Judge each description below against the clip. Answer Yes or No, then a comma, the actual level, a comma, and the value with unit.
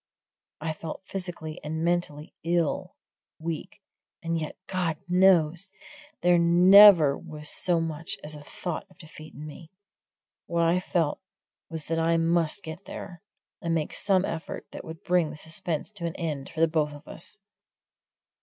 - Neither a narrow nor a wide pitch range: No, narrow, 2.1 semitones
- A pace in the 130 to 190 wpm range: Yes, average, 155 wpm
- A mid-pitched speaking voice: Yes, medium, 165 Hz